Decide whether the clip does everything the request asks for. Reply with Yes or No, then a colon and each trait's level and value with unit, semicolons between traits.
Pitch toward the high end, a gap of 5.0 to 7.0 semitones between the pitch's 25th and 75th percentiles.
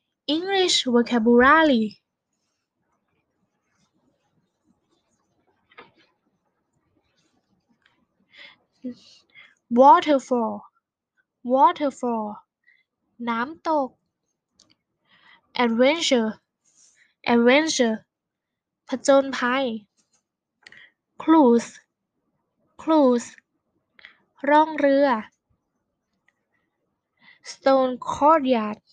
No: very high, 260 Hz; average, 4.4 semitones